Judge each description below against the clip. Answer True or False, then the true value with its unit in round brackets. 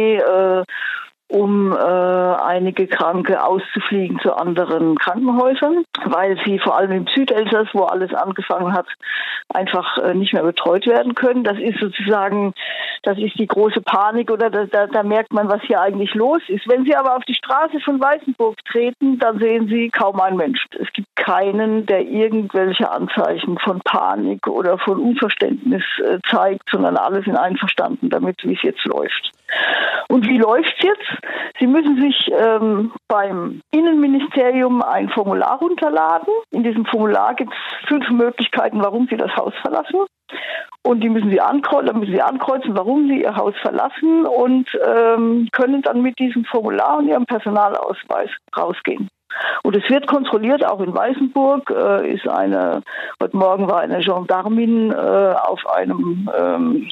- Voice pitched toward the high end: True (225 Hz)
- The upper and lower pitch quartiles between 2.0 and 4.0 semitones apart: False (5.2 semitones)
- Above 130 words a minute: True (160 wpm)